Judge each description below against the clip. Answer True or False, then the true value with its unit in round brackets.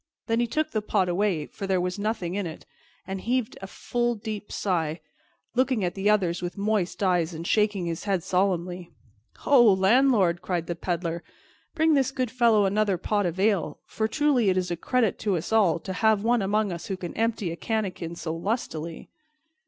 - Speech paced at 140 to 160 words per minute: False (195 wpm)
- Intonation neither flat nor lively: True (3.8 semitones)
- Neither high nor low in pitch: False (195 Hz)